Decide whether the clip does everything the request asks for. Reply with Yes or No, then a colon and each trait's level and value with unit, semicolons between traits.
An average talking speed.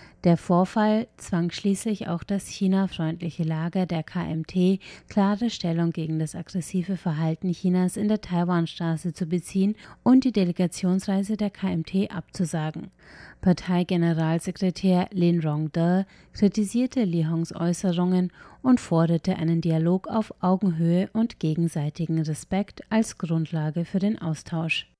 No: slow, 120 wpm